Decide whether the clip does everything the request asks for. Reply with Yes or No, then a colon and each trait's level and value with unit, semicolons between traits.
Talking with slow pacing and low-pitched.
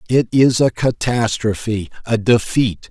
Yes: slow, 125 wpm; low, 115 Hz